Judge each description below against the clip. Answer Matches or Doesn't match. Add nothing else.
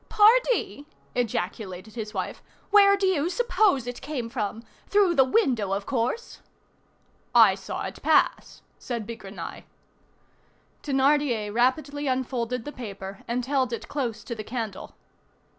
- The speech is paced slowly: Matches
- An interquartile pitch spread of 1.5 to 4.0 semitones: Doesn't match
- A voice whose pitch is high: Matches